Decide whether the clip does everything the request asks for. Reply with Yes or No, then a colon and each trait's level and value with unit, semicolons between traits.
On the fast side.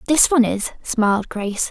No: average, 175 wpm